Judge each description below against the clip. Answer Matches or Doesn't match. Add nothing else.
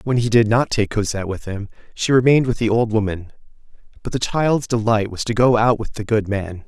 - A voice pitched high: Doesn't match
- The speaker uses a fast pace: Matches